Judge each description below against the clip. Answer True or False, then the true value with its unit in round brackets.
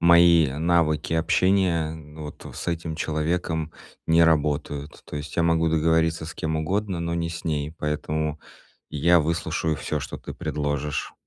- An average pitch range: False (1.7 semitones)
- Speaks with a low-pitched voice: True (80 Hz)